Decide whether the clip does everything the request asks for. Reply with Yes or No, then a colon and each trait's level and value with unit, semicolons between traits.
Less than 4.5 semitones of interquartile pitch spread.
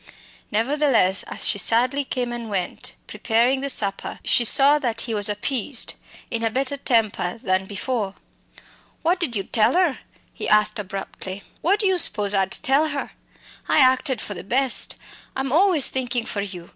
No: average, 5.0 semitones